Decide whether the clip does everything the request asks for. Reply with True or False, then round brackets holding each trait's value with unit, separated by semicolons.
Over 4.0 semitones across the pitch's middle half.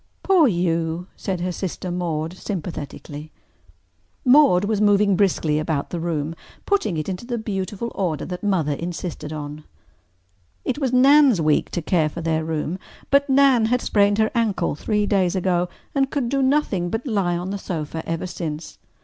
True (5.2 semitones)